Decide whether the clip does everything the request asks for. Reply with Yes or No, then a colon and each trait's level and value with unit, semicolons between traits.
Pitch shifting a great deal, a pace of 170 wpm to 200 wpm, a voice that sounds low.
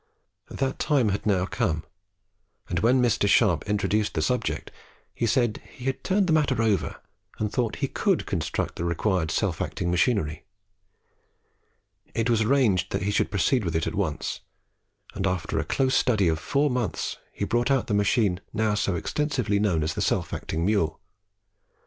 Yes: wide, 5.7 semitones; average, 175 wpm; low, 105 Hz